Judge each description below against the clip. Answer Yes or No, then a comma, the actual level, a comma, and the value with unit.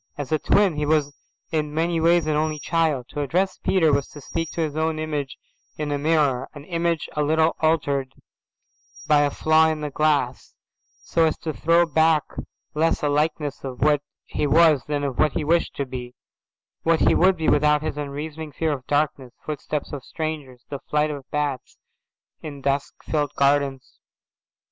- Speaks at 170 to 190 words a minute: Yes, average, 180 wpm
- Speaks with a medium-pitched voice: Yes, medium, 150 Hz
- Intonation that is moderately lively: No, narrow, 2.0 semitones